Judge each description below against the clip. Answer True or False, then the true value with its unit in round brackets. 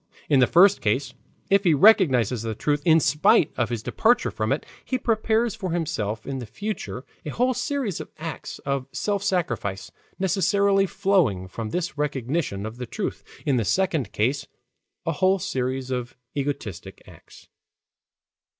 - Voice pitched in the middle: True (145 Hz)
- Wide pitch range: True (7.9 semitones)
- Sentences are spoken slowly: False (160 wpm)